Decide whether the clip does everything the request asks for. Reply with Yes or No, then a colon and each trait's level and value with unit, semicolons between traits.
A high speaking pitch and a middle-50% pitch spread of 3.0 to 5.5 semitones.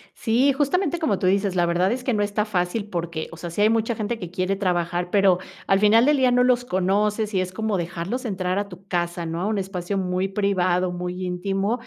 Yes: high, 195 Hz; average, 3.5 semitones